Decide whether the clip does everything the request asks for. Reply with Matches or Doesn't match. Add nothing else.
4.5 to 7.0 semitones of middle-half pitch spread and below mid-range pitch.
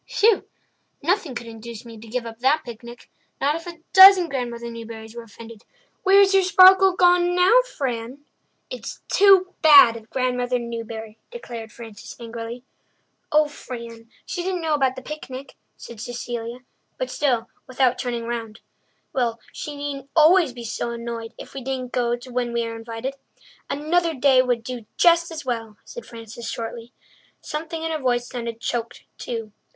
Doesn't match